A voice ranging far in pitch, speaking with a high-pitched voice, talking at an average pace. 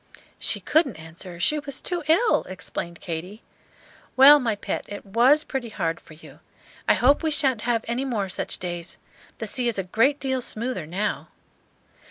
Yes: wide, 6.6 semitones; high, 235 Hz; average, 175 wpm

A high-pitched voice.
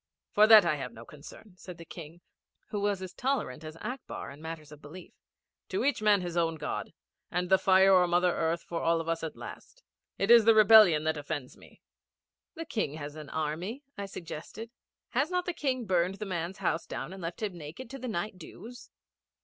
No: medium, 180 Hz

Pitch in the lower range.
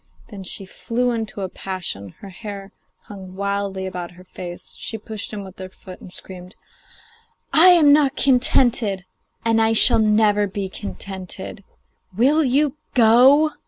No: high, 205 Hz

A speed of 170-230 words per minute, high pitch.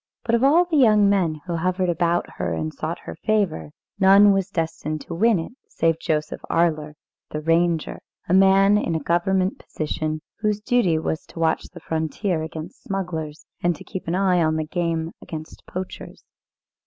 No: average, 180 wpm; medium, 170 Hz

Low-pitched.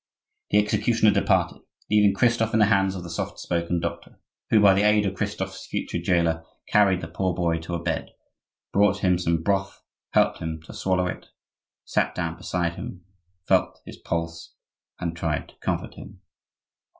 Yes: very low, 90 Hz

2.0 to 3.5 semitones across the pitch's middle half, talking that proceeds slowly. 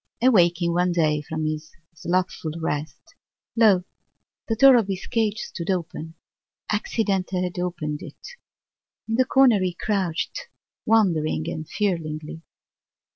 No: average, 4.8 semitones; slow, 125 wpm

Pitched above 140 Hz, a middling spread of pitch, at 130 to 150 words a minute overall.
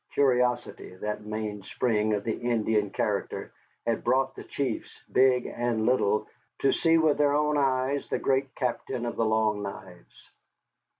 No: low, 120 Hz; average, 3.8 semitones; average, 145 wpm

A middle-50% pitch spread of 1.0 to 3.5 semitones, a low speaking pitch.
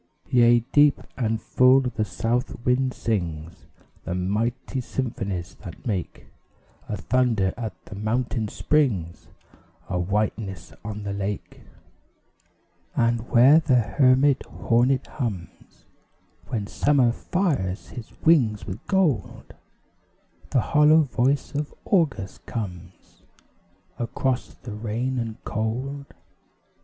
No: average, 4.2 semitones; low, 115 Hz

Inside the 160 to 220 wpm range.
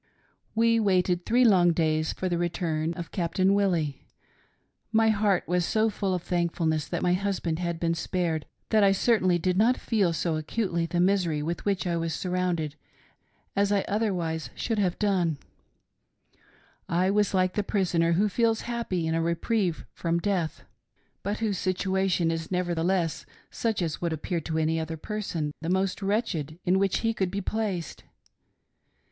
Yes: average, 170 wpm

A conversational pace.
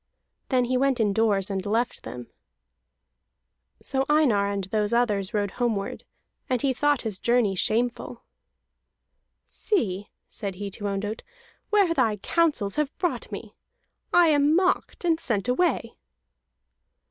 No: slow, 130 wpm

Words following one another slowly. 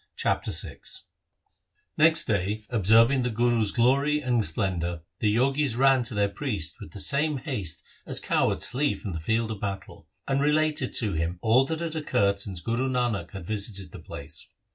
No: average, 180 wpm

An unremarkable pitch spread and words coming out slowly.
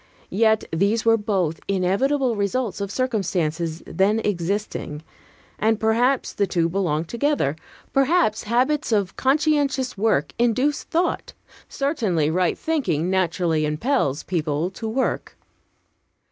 No: wide, 6.7 semitones; slow, 115 wpm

